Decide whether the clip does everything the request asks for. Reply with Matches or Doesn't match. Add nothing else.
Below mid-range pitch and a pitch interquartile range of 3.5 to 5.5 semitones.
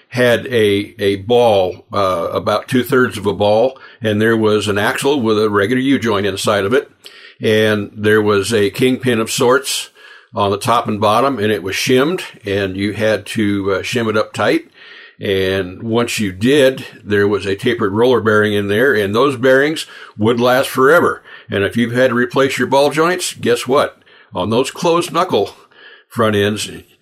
Matches